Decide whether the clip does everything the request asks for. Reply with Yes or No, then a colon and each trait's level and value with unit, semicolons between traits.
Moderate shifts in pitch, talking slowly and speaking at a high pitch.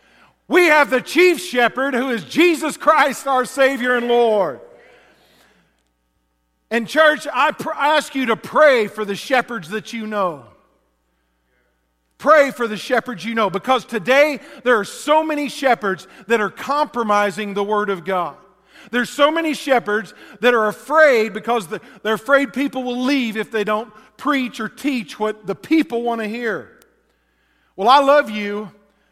No: average, 4.9 semitones; average, 160 wpm; high, 235 Hz